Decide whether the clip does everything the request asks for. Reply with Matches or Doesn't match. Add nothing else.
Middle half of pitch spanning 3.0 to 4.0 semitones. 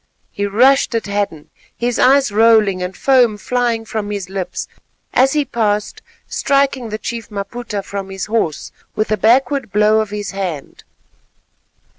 Matches